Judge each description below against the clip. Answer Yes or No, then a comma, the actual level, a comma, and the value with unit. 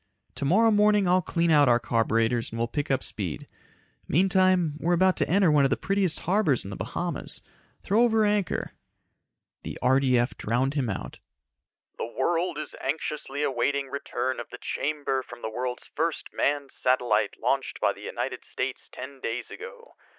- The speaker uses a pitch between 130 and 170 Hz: Yes, medium, 140 Hz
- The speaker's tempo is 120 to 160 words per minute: No, average, 170 wpm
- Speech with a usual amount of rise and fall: No, wide, 6.5 semitones